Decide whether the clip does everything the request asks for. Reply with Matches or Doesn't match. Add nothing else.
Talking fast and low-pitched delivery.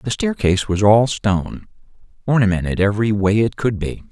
Doesn't match